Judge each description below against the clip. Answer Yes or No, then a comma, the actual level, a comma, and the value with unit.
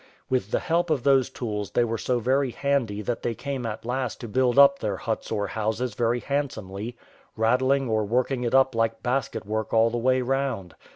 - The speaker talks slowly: No, fast, 205 wpm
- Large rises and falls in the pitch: No, average, 3.1 semitones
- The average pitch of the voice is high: No, low, 120 Hz